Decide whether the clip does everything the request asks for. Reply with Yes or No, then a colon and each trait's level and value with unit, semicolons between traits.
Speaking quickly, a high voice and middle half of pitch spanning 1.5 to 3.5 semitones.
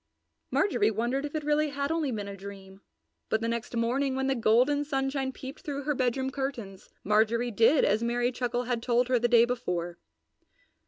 No: average, 190 wpm; high, 245 Hz; average, 3.1 semitones